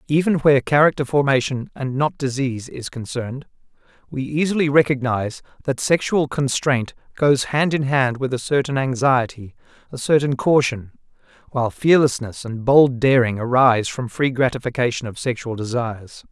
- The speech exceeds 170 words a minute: No, average, 140 wpm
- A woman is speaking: No, male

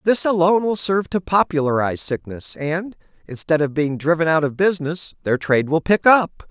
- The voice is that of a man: Yes, male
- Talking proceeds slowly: No, average, 185 wpm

